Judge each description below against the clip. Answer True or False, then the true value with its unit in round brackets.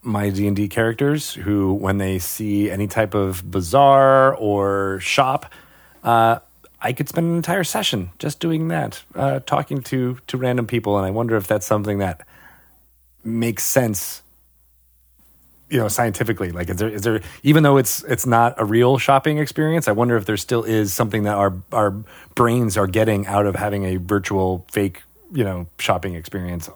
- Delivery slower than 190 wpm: True (180 wpm)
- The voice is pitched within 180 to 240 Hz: False (105 Hz)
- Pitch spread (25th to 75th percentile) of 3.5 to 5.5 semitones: True (4.2 semitones)